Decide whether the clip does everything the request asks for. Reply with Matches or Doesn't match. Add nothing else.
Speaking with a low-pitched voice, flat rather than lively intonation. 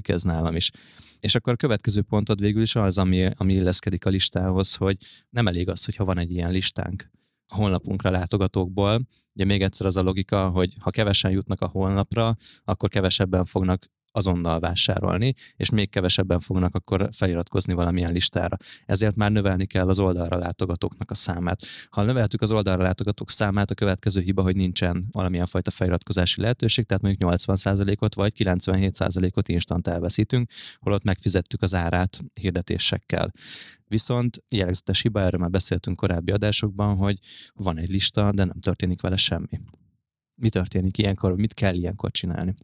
Matches